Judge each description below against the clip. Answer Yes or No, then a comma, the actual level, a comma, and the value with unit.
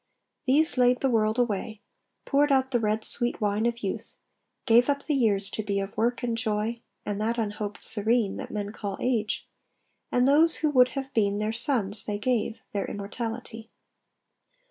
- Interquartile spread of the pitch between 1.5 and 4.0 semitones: Yes, average, 3.1 semitones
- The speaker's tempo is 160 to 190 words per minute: Yes, average, 175 wpm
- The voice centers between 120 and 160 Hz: No, high, 225 Hz